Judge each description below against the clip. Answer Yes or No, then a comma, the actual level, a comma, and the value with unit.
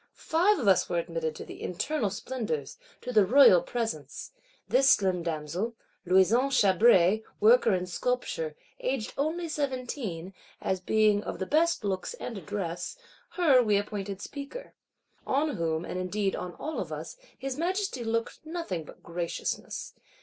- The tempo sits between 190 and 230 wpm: No, average, 150 wpm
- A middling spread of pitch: No, wide, 6.9 semitones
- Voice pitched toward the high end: Yes, high, 215 Hz